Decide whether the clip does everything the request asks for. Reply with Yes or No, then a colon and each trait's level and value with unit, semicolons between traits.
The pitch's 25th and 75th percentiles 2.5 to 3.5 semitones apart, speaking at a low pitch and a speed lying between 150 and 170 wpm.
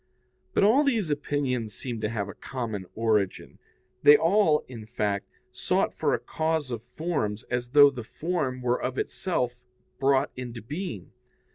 No: average, 5.0 semitones; low, 125 Hz; average, 155 wpm